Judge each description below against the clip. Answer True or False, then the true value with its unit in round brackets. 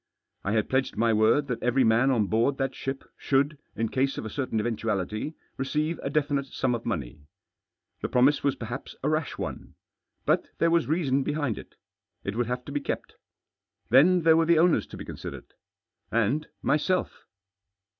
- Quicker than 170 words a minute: True (185 wpm)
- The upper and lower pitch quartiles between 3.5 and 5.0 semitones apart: True (4.5 semitones)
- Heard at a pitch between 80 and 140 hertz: True (135 Hz)